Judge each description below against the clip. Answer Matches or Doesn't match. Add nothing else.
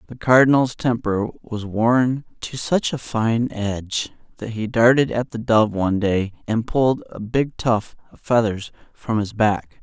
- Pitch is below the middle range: Matches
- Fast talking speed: Doesn't match